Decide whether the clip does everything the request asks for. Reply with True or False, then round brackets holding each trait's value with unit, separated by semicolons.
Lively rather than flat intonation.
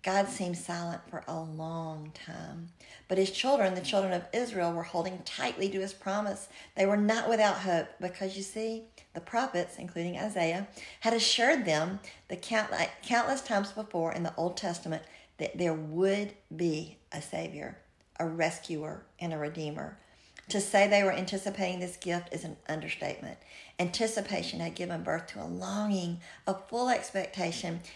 False (3.0 semitones)